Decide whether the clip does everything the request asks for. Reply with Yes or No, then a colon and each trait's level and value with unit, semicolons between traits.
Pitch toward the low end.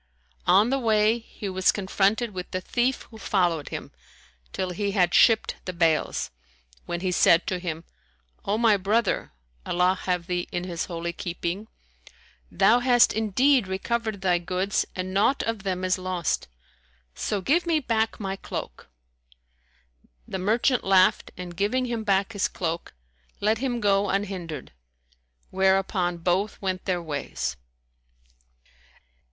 No: high, 195 Hz